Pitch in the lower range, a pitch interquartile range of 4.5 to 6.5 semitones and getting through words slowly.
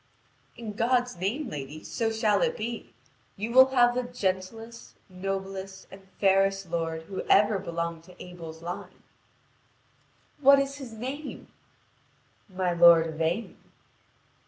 No: high, 195 Hz; average, 5.2 semitones; slow, 130 wpm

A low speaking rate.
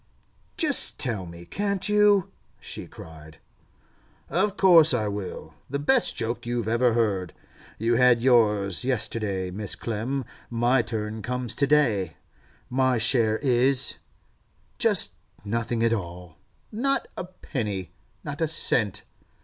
Yes: slow, 125 wpm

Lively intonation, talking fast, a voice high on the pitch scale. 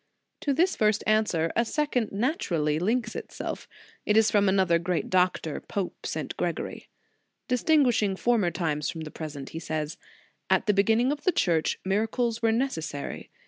No: wide, 6.0 semitones; average, 160 wpm; high, 205 Hz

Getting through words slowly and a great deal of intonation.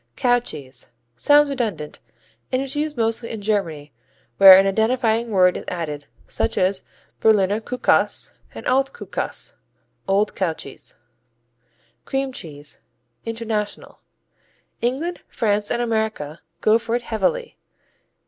No: slow, 120 wpm; average, 4.6 semitones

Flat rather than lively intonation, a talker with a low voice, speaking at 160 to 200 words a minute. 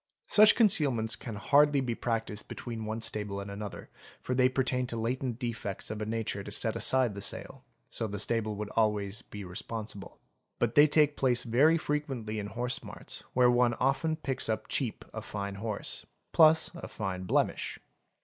No: average, 3.8 semitones; low, 115 Hz; average, 180 wpm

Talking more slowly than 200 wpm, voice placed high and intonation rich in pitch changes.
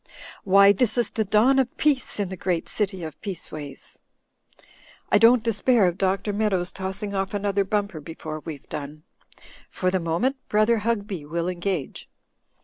No: average, 155 wpm; high, 195 Hz; average, 3.6 semitones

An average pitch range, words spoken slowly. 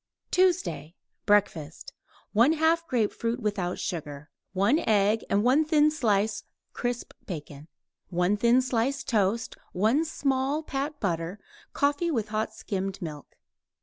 No: wide, 6.3 semitones; slow, 115 wpm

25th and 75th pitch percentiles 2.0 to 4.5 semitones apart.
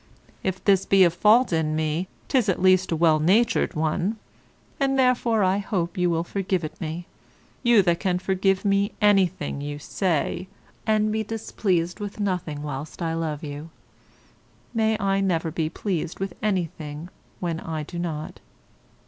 Yes: average, 3.8 semitones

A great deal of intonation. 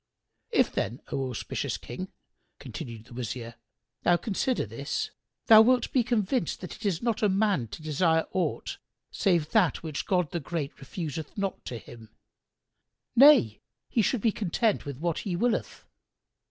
Yes: wide, 7.8 semitones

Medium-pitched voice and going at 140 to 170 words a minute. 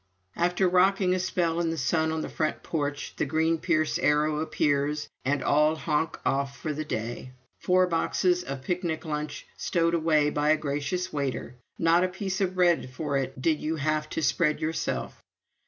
No: medium, 155 Hz; average, 180 wpm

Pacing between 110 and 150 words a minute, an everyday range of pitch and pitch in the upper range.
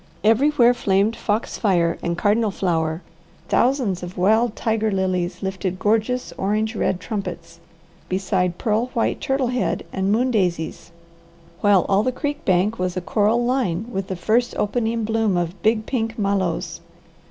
Yes: average, 145 wpm; average, 3.8 semitones; high, 205 Hz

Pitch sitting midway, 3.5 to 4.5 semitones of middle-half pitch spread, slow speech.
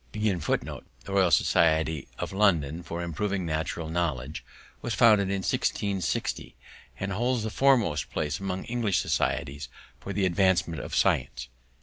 No: very low, 95 Hz; average, 4.2 semitones; slow, 130 wpm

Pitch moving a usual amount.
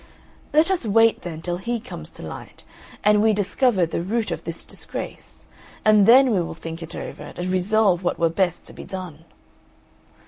Yes: average, 4.4 semitones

